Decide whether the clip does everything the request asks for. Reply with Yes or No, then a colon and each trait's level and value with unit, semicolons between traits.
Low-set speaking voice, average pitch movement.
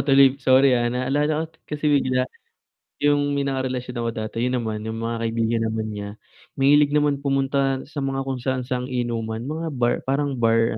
Yes: low, 130 Hz; average, 3.0 semitones